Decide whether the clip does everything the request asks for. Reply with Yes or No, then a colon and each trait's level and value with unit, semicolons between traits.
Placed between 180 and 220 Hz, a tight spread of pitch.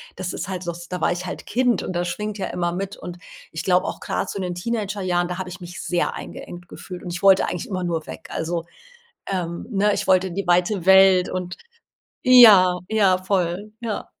Yes: medium, 185 Hz; narrow, 1.9 semitones